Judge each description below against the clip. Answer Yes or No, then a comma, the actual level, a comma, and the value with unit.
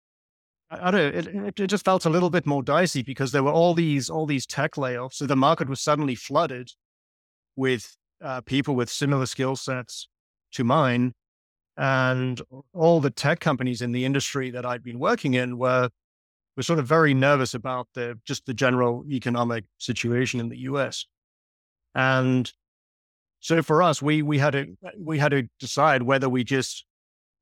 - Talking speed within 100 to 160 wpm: No, average, 175 wpm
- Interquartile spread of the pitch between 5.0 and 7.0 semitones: No, average, 3.2 semitones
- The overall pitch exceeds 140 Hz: No, low, 130 Hz